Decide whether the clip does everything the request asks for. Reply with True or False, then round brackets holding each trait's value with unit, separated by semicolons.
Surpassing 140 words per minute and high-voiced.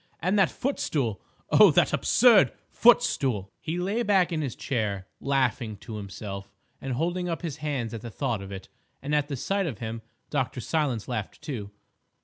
False (175 wpm; 135 Hz)